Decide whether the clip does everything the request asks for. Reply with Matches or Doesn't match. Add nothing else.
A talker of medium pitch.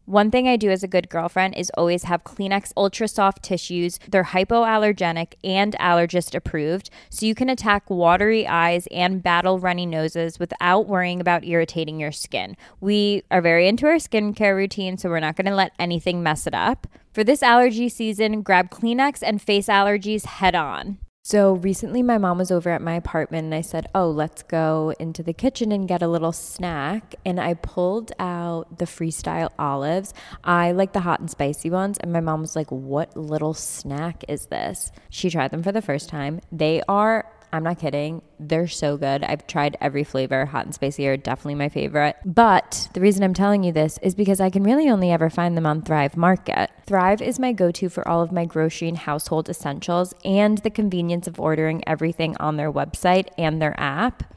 Matches